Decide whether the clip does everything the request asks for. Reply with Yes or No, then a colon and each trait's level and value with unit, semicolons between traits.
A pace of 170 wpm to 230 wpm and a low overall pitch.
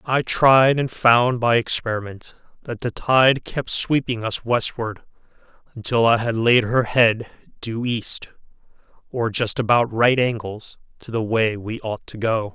No: average, 160 wpm; low, 115 Hz